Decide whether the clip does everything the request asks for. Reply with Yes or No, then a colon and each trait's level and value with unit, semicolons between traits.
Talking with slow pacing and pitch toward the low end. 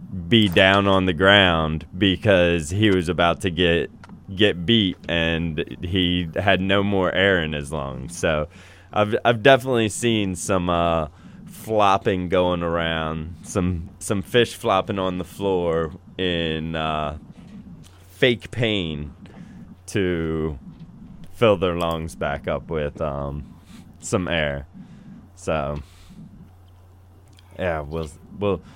Yes: slow, 120 wpm; very low, 90 Hz